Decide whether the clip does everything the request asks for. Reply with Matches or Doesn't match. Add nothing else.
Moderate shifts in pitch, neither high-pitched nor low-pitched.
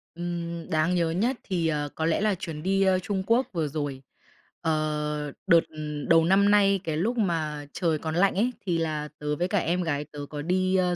Matches